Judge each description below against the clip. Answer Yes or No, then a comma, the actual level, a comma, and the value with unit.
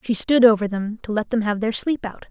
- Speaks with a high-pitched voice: Yes, high, 220 Hz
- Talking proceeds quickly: Yes, fast, 285 wpm